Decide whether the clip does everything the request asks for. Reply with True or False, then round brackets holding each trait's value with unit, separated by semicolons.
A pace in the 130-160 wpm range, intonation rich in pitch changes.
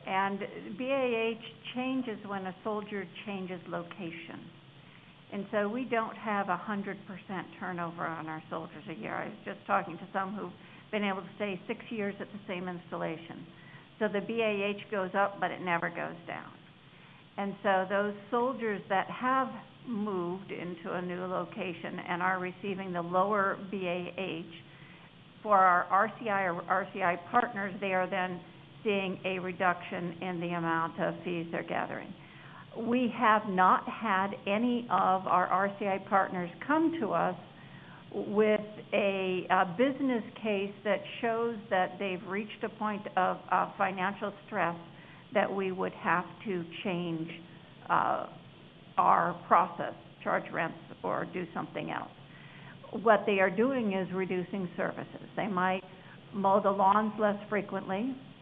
False (145 wpm; 2.8 semitones)